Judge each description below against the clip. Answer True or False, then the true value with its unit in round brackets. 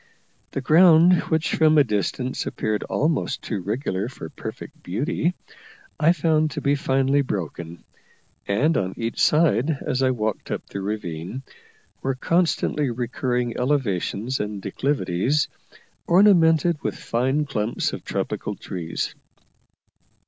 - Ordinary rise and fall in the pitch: False (6.5 semitones)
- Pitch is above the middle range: False (130 Hz)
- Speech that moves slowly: True (125 wpm)